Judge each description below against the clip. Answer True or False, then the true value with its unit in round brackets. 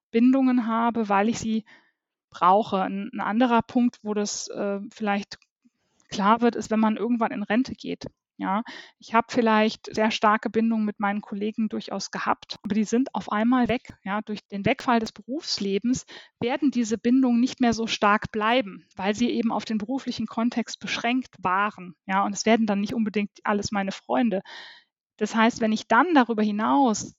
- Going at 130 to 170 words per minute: False (180 wpm)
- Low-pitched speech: False (220 Hz)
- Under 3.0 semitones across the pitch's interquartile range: True (2.5 semitones)